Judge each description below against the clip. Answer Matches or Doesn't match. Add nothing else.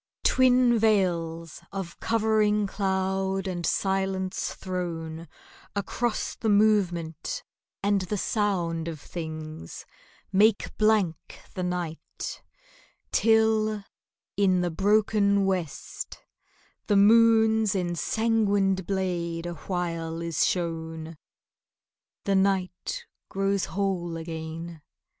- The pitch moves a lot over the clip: Doesn't match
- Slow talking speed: Matches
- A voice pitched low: Doesn't match